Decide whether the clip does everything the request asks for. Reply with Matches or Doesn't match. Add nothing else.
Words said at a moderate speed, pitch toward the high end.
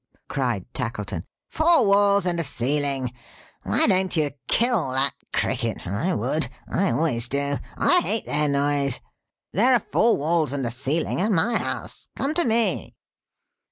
Doesn't match